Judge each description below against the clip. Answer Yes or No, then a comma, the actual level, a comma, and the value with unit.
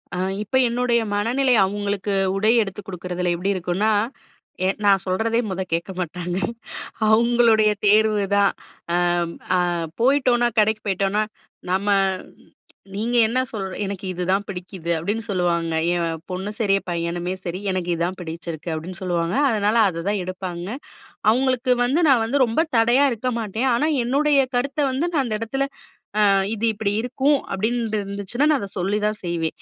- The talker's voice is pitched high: Yes, high, 205 Hz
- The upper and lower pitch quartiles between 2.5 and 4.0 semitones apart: No, average, 4.6 semitones